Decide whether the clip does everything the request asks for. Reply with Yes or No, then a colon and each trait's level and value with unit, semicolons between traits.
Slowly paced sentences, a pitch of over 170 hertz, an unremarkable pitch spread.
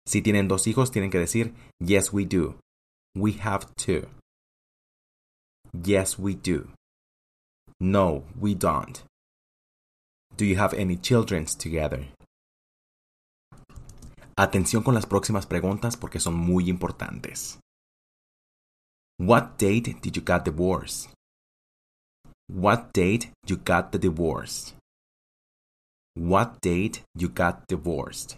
No: slow, 110 wpm; very low, 95 Hz; average, 3.5 semitones